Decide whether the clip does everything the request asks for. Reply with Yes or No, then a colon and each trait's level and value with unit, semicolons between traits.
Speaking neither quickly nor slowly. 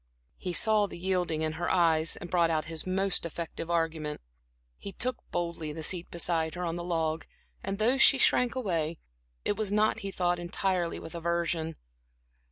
Yes: average, 175 wpm